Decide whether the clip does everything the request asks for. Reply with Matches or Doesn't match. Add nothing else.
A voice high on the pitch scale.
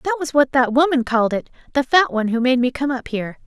Matches